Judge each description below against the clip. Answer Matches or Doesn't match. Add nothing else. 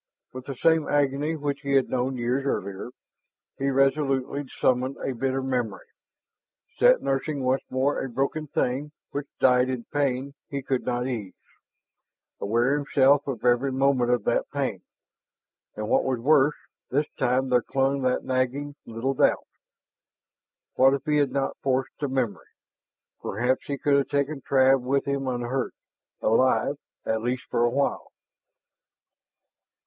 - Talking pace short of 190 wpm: Matches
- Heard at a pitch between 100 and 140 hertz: Matches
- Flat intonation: Matches